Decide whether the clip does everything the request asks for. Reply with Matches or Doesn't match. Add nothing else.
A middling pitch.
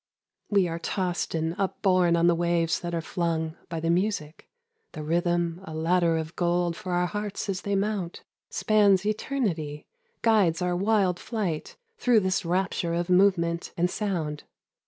Matches